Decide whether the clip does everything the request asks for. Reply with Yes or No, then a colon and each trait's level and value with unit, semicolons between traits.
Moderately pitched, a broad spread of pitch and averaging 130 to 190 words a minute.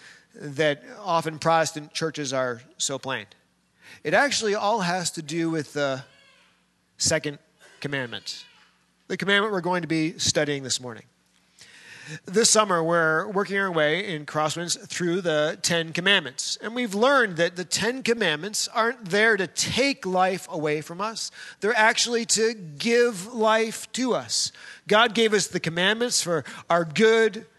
Yes: medium, 180 Hz; wide, 5.8 semitones; average, 150 wpm